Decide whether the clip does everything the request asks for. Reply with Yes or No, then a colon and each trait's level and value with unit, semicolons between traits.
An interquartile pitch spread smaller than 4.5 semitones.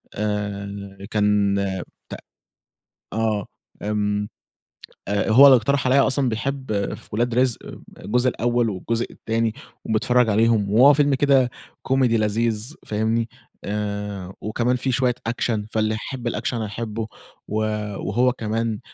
Yes: average, 3.0 semitones